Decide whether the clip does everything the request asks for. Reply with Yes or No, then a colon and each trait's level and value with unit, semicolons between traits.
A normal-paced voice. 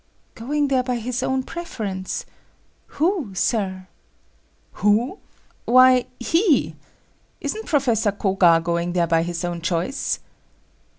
No: slow, 110 wpm